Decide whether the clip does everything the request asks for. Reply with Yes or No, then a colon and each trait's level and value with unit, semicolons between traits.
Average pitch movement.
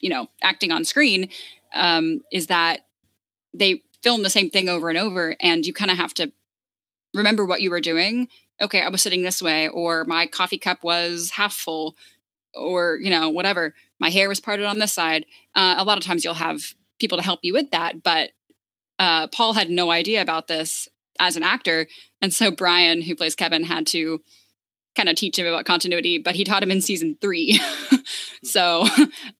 Yes: average, 3.6 semitones